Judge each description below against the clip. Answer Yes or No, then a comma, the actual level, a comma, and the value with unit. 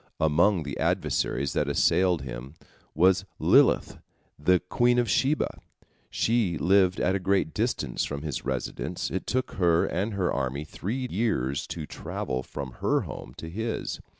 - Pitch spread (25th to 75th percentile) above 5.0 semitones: Yes, wide, 5.6 semitones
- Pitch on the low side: Yes, very low, 90 Hz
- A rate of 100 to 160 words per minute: Yes, average, 150 wpm